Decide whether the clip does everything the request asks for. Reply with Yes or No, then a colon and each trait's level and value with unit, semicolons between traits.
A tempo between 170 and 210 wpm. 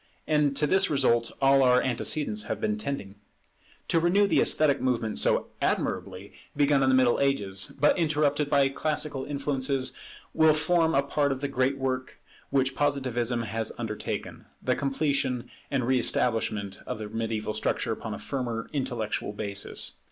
No: average, 160 wpm